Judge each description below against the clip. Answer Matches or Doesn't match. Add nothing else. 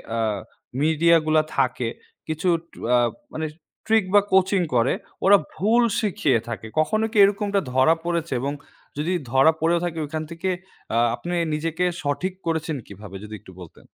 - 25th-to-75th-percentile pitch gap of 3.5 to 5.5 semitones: Matches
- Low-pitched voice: Doesn't match